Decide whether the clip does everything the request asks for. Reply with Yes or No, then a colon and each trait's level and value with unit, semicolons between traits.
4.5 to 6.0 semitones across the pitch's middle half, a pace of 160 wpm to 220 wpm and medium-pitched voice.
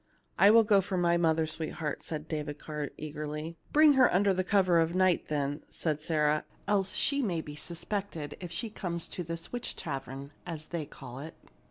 No: average, 3.7 semitones; average, 190 wpm; medium, 165 Hz